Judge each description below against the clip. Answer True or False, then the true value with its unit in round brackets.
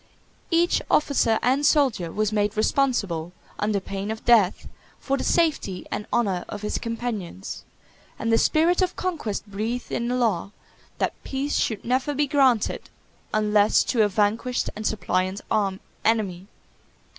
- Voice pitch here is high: True (220 Hz)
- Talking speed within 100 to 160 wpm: True (145 wpm)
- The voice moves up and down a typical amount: True (4.5 semitones)